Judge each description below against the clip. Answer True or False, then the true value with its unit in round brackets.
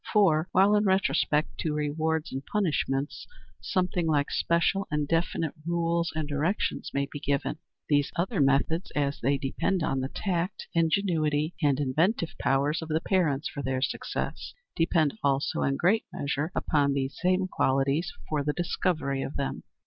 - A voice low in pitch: False (155 Hz)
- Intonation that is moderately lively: True (3.5 semitones)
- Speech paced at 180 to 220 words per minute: False (155 wpm)